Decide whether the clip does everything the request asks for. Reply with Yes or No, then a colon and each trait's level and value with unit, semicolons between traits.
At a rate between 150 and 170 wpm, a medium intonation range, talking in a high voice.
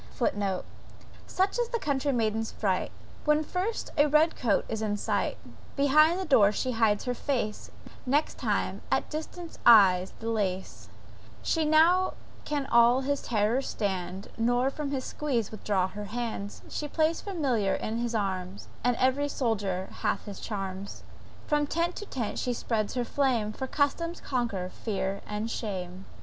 No: average, 160 wpm; wide, 6.0 semitones; high, 235 Hz